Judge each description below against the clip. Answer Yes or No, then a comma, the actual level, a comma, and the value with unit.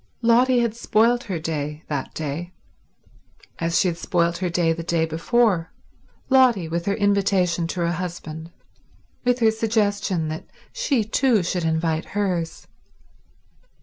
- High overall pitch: No, medium, 180 Hz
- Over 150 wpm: No, slow, 135 wpm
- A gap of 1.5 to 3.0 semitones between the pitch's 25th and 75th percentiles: No, average, 4.9 semitones